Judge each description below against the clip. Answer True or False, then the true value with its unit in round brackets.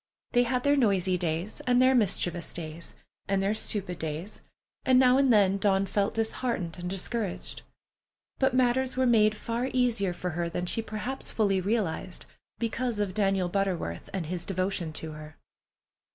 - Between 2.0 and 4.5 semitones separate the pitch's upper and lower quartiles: False (5.1 semitones)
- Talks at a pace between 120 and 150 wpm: False (165 wpm)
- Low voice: False (200 Hz)